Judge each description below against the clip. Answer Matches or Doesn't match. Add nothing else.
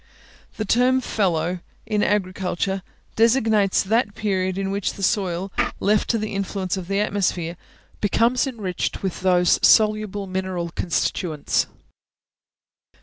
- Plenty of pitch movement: Doesn't match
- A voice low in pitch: Doesn't match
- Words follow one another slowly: Matches